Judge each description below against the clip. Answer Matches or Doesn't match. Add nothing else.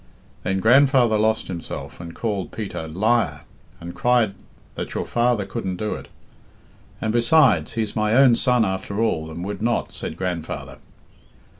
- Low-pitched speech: Matches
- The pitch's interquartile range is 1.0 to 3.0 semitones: Doesn't match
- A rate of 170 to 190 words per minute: Doesn't match